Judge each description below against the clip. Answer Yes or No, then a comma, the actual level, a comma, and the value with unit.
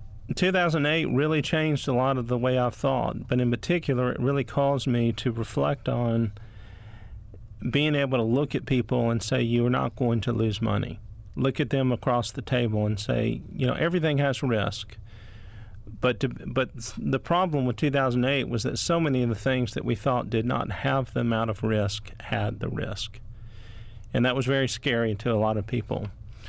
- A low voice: Yes, low, 120 Hz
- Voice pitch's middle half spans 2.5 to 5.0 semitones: Yes, average, 3.7 semitones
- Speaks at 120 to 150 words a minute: No, average, 195 wpm